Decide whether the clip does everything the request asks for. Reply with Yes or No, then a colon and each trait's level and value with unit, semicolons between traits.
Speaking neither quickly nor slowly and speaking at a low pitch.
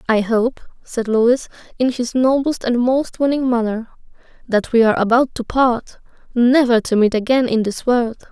No: average, 175 wpm; high, 240 Hz